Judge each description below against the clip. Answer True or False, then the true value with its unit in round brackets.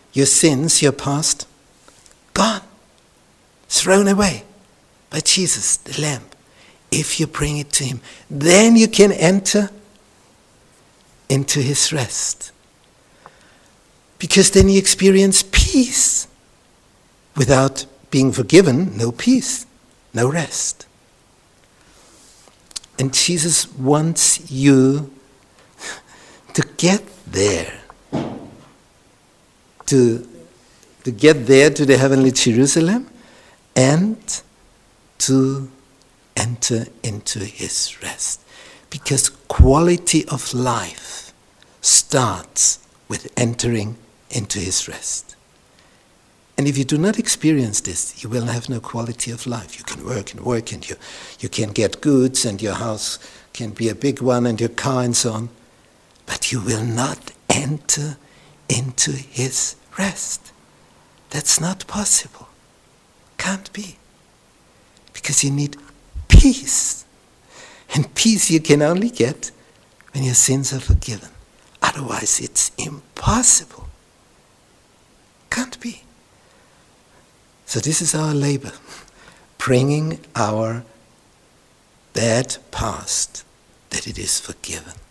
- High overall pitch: False (135 Hz)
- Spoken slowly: True (105 wpm)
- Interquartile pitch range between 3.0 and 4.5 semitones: False (5.4 semitones)